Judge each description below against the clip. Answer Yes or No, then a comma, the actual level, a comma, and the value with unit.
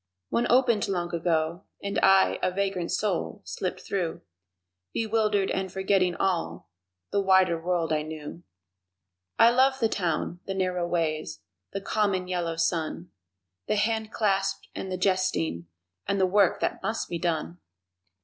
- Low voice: No, medium, 185 Hz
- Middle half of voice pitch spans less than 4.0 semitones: Yes, average, 2.9 semitones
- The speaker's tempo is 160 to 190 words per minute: No, average, 140 wpm